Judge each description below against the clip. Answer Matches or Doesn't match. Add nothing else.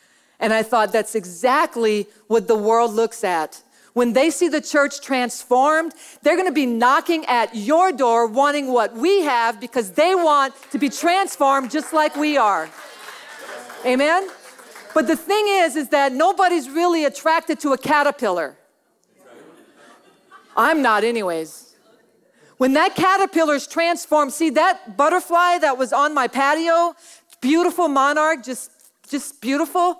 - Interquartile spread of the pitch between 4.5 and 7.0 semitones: Matches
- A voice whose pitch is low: Doesn't match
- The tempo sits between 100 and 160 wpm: Matches